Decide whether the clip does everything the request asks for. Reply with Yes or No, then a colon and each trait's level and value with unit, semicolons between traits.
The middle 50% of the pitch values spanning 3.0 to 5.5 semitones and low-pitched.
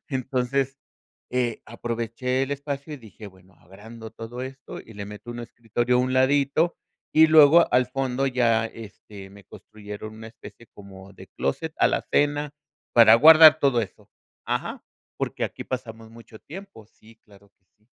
Yes: average, 3.7 semitones; low, 120 Hz